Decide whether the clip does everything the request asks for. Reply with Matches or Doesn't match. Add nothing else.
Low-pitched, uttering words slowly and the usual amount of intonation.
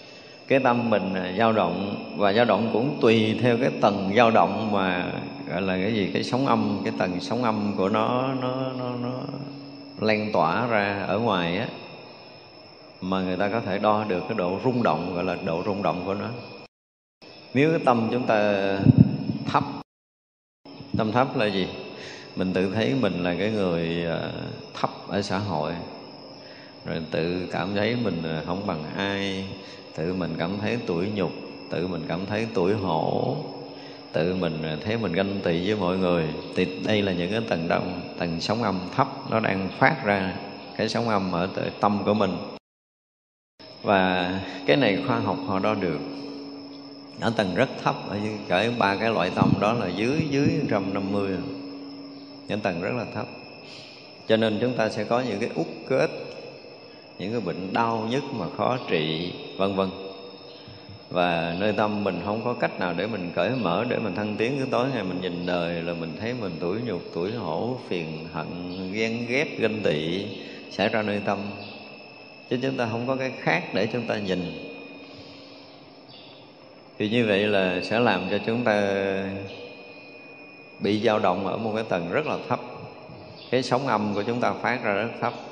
Doesn't match